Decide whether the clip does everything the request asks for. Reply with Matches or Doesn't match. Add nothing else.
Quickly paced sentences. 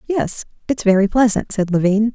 Doesn't match